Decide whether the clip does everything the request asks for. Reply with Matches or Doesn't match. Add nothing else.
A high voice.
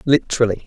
Doesn't match